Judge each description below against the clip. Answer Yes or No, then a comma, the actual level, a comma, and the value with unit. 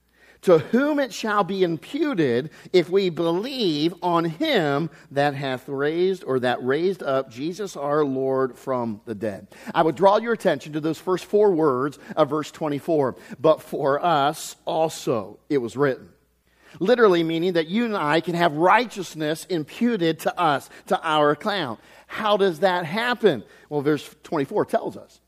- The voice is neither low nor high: Yes, medium, 165 Hz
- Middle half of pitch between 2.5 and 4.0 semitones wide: No, average, 5.0 semitones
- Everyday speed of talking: Yes, average, 160 wpm